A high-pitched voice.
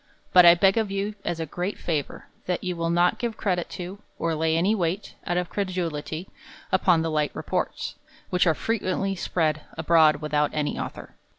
No: medium, 175 Hz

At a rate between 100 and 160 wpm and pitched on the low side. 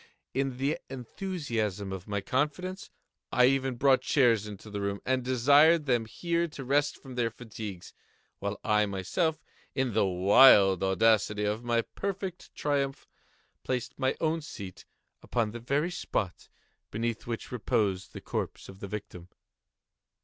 Yes: average, 140 wpm; low, 120 Hz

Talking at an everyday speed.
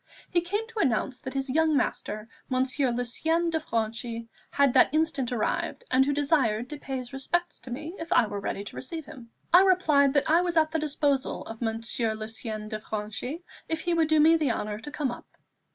No: fast, 210 wpm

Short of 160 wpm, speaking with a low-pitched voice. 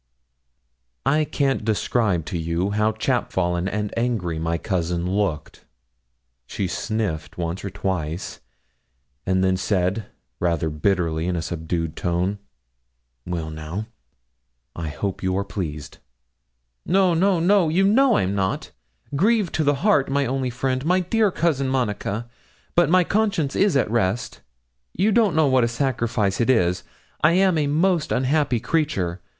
Yes: average, 145 wpm; low, 110 Hz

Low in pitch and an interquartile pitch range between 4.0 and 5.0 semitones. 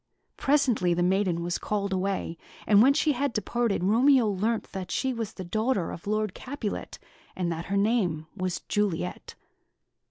No: high, 205 Hz; average, 4.4 semitones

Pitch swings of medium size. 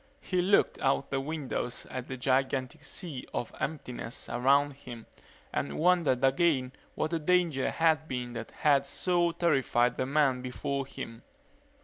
Yes: average, 3.8 semitones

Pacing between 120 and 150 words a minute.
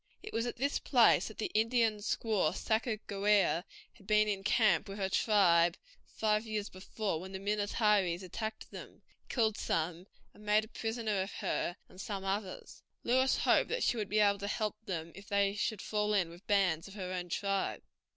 No: average, 190 wpm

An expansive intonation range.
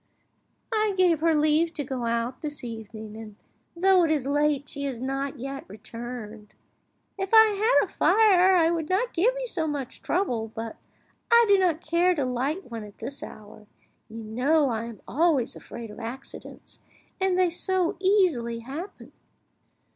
Yes: wide, 7.5 semitones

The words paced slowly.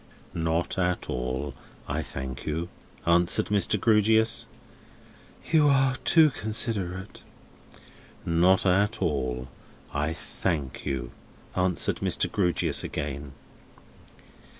Yes: slow, 95 wpm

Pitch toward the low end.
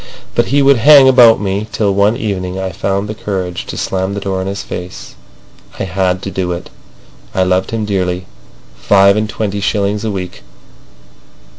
Yes: low, 100 Hz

